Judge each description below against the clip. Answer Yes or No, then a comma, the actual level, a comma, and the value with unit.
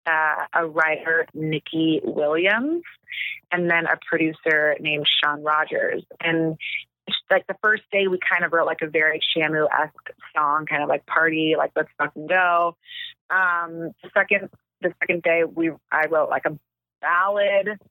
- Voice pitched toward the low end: No, medium, 165 Hz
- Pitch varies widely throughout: No, average, 2.9 semitones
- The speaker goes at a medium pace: Yes, average, 160 wpm